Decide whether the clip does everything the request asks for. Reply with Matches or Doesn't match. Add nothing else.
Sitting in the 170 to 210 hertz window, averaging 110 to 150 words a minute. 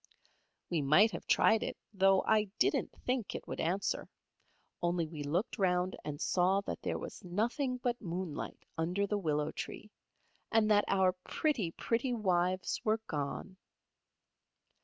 Matches